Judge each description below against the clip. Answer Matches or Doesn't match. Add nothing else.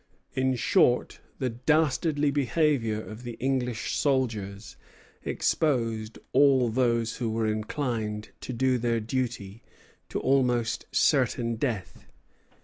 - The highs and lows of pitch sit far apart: Doesn't match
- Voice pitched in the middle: Doesn't match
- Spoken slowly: Matches